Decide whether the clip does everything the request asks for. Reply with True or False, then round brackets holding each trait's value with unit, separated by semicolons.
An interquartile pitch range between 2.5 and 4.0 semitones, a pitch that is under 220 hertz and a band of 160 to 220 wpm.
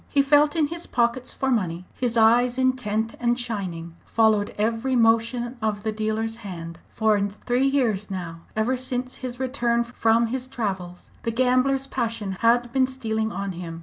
False (3.2 semitones; 230 Hz; 165 wpm)